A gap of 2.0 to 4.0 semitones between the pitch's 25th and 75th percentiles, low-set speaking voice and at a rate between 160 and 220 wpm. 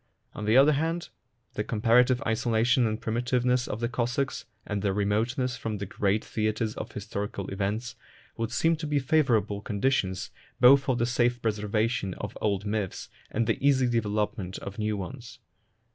Yes: average, 3.2 semitones; low, 115 Hz; average, 165 wpm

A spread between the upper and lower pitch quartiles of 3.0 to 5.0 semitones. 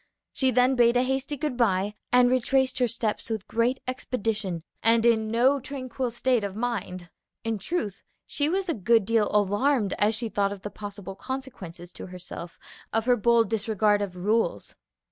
Yes: average, 3.8 semitones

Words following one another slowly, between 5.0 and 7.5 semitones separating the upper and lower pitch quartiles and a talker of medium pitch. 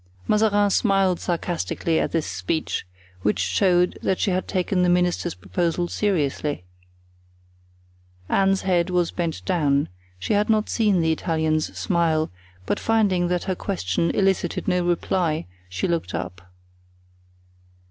No: slow, 125 wpm; average, 3.3 semitones; medium, 175 Hz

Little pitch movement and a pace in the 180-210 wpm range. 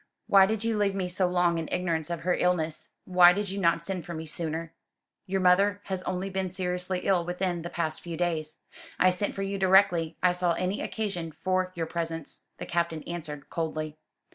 Yes: narrow, 2.3 semitones; average, 200 wpm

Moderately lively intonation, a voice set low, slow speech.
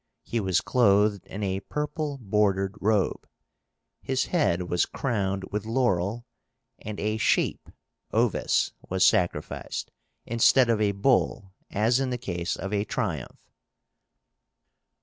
Yes: average, 3.6 semitones; low, 105 Hz; slow, 125 wpm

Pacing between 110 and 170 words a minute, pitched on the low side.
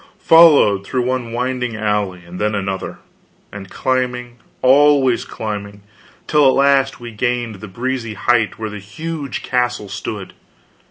Yes: average, 140 wpm; low, 120 Hz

